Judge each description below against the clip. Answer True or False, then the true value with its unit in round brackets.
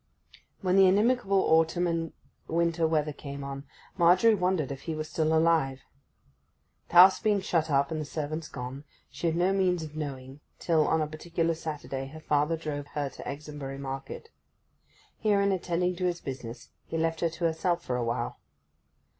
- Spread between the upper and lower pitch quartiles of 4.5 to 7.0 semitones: False (3.5 semitones)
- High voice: False (160 Hz)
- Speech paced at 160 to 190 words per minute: True (175 wpm)